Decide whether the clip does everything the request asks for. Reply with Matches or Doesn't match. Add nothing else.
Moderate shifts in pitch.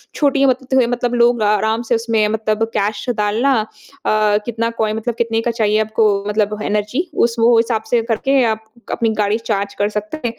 Doesn't match